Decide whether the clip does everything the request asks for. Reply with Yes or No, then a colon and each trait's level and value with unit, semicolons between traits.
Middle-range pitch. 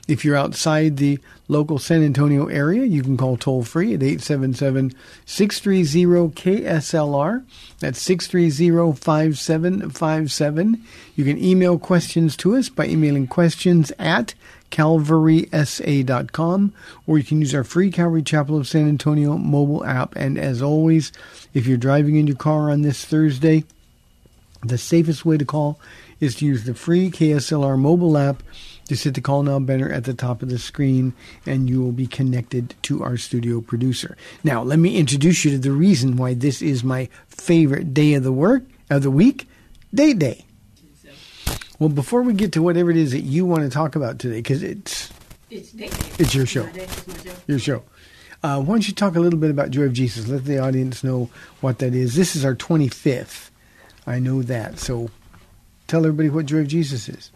Yes: medium, 150 Hz